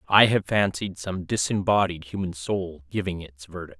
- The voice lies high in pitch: No, very low, 90 Hz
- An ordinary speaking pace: Yes, average, 160 wpm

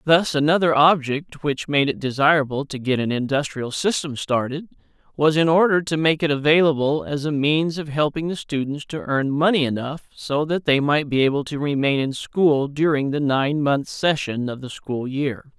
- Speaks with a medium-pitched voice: Yes, medium, 145 Hz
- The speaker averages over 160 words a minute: Yes, average, 195 wpm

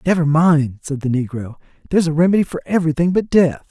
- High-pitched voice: No, medium, 160 Hz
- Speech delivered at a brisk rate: No, average, 195 wpm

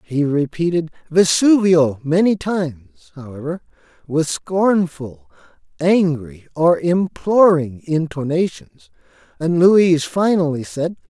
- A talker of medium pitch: Yes, medium, 160 Hz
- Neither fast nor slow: No, slow, 85 wpm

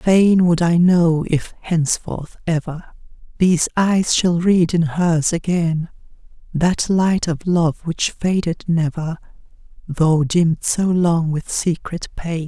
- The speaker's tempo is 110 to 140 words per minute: Yes, slow, 135 wpm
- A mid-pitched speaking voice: Yes, medium, 170 Hz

